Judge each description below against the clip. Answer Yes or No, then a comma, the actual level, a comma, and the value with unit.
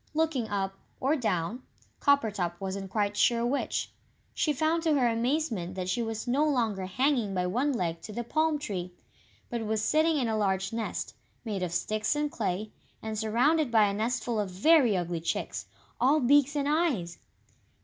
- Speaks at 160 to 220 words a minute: Yes, average, 175 wpm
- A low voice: No, high, 225 Hz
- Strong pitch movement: Yes, wide, 6.6 semitones